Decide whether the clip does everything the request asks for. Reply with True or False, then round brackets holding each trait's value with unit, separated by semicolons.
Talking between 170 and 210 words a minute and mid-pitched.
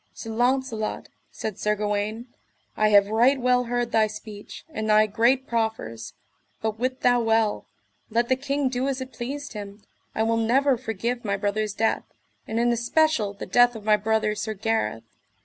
False (175 wpm; 225 Hz)